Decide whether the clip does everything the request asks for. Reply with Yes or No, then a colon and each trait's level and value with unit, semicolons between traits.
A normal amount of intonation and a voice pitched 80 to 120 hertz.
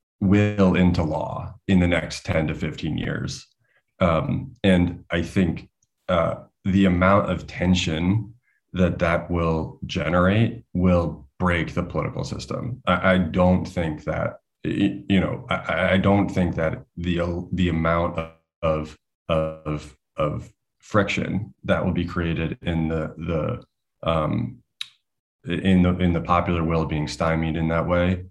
No: narrow, 2.1 semitones; very low, 85 Hz